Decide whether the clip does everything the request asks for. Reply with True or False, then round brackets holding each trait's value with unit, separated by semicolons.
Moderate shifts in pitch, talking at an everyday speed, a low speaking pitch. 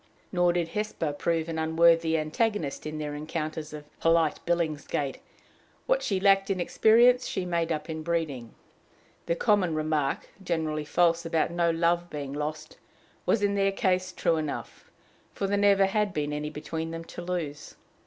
False (3.0 semitones; 165 wpm; 165 Hz)